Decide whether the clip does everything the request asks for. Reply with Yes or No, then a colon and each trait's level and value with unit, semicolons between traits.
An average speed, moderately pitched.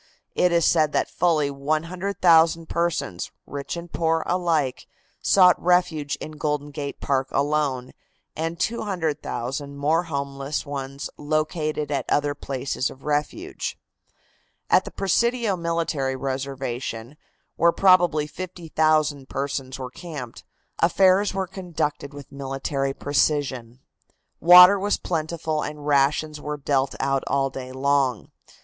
No: slow, 120 wpm; medium, 150 Hz